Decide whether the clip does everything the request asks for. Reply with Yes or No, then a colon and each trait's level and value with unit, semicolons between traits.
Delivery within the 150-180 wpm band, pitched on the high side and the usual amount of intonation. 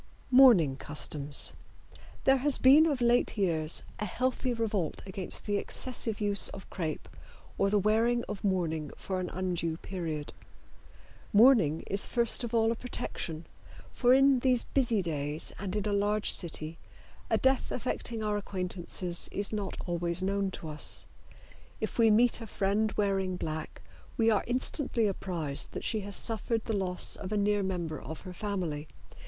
Yes: average, 160 wpm; high, 200 Hz; average, 4.7 semitones